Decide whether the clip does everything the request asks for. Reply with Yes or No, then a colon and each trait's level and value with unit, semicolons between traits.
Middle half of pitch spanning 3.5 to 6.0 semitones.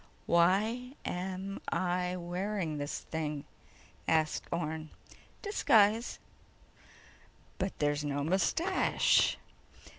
Yes: average, 4.4 semitones